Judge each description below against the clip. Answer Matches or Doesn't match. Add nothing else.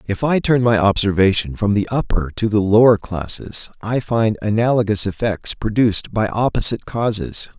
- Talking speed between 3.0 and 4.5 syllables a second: Doesn't match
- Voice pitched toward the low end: Matches